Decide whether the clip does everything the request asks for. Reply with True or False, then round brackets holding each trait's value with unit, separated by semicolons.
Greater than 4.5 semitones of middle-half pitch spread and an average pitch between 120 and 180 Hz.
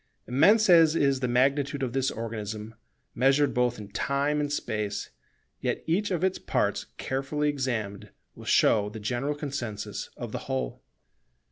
True (4.9 semitones; 135 Hz)